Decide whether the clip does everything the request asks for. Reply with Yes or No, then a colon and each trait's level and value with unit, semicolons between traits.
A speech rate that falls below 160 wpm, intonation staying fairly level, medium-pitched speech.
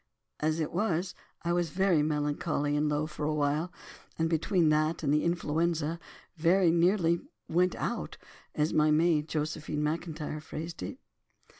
Yes: average, 145 wpm; narrow, 2.1 semitones; medium, 160 Hz